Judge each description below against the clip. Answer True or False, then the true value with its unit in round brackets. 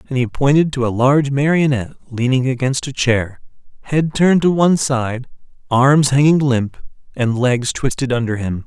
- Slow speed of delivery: False (165 wpm)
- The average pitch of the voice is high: False (130 Hz)